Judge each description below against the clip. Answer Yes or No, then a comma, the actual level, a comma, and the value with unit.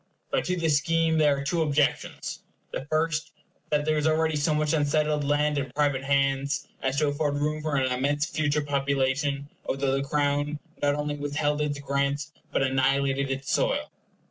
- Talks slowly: No, average, 175 wpm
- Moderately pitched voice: Yes, medium, 145 Hz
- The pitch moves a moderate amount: No, narrow, 1.5 semitones